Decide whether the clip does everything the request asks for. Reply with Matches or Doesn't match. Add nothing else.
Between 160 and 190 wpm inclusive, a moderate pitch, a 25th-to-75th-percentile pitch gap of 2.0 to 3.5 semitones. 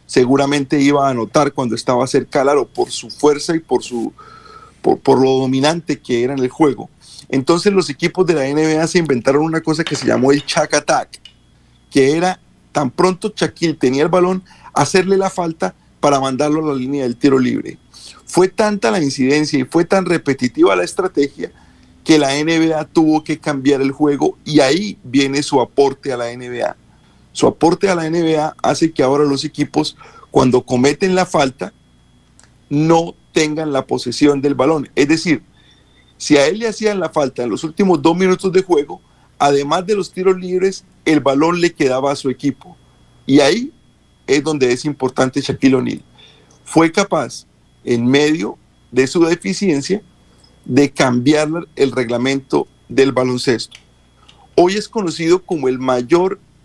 Doesn't match